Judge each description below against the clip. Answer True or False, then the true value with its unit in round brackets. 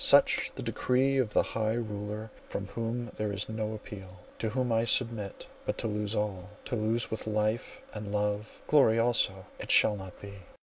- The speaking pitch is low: True (110 Hz)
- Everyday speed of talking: True (180 wpm)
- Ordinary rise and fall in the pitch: False (2.0 semitones)